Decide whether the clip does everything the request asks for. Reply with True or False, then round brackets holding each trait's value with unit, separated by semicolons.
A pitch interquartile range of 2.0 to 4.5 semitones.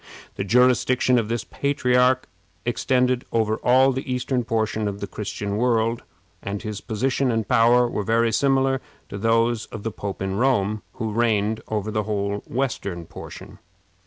True (3.1 semitones)